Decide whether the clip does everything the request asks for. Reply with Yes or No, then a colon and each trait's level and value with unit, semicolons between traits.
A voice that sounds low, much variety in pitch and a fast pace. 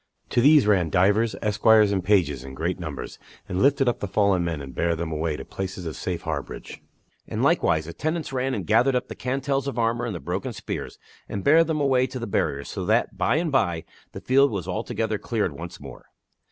Yes: low, 105 Hz; wide, 7.0 semitones; fast, 215 wpm